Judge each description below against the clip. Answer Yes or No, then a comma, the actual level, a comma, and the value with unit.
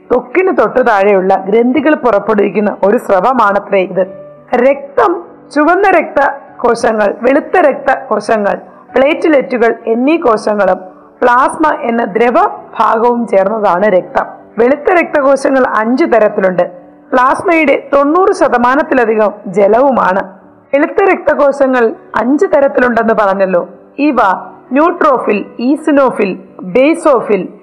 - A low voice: No, very high, 250 Hz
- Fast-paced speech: No, average, 90 wpm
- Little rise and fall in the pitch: No, wide, 5.5 semitones